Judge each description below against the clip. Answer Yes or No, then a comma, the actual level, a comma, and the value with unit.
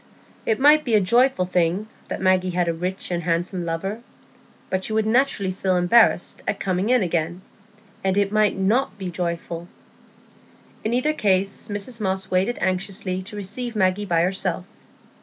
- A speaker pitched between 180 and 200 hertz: Yes, high, 190 Hz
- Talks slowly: No, average, 165 wpm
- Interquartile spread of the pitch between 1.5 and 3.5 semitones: Yes, average, 3.0 semitones